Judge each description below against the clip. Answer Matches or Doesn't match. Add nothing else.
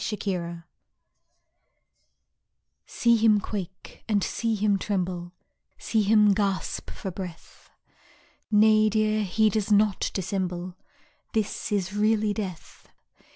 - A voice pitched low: Doesn't match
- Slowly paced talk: Matches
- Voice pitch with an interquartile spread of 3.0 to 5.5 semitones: Doesn't match